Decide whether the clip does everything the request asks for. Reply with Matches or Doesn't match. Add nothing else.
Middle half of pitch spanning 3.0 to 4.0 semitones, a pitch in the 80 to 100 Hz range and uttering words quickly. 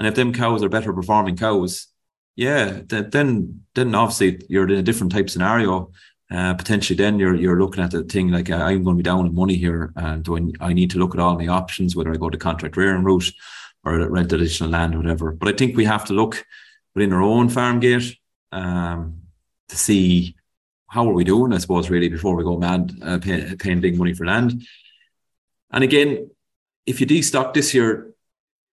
Matches